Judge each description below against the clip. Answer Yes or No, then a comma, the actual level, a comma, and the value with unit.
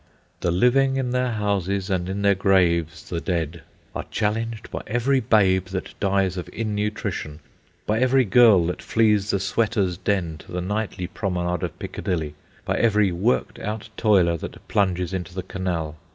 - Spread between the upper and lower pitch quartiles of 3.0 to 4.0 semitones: Yes, average, 3.4 semitones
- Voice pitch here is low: Yes, very low, 95 Hz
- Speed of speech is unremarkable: Yes, average, 165 wpm